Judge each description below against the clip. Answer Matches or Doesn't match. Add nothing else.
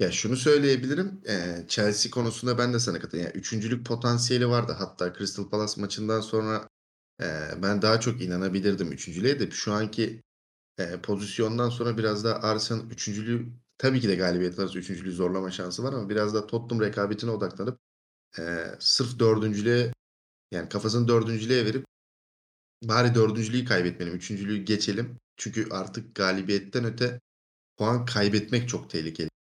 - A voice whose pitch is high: Doesn't match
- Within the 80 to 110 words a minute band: Doesn't match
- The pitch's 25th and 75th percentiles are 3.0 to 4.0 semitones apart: Matches